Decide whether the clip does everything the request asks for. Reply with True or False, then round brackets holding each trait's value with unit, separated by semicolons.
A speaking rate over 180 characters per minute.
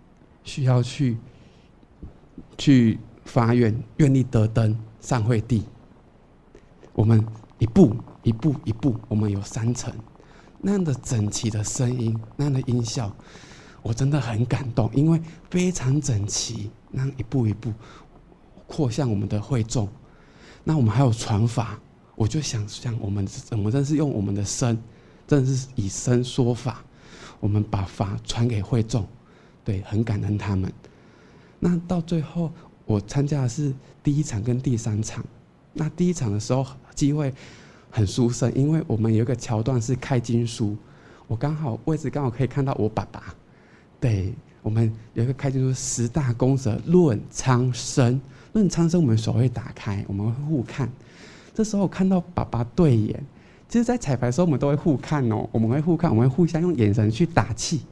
True (240 characters per minute)